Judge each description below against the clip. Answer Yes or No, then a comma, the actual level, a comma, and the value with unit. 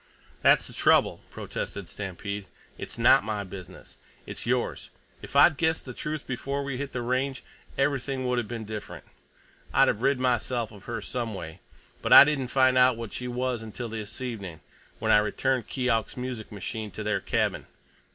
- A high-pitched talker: No, low, 120 Hz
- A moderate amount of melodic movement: Yes, average, 3.5 semitones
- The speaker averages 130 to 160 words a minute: No, average, 180 wpm